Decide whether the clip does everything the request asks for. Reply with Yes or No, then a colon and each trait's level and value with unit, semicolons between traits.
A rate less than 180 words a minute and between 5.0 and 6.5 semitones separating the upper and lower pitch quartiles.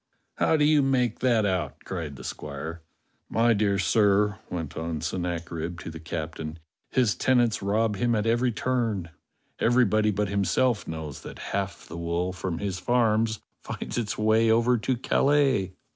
Yes: average, 160 wpm; wide, 5.5 semitones